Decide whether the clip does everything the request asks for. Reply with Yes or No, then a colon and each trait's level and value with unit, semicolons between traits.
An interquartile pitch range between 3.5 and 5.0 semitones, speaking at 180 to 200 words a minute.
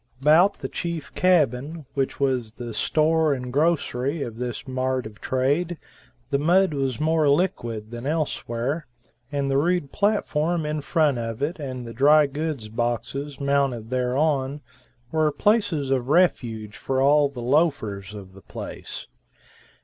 No: average, 4.1 semitones; average, 145 wpm